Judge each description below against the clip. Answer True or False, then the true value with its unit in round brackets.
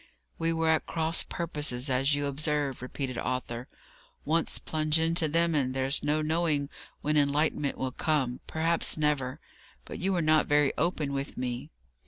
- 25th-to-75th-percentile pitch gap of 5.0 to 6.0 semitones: False (2.9 semitones)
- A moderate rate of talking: True (160 wpm)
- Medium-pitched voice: True (150 Hz)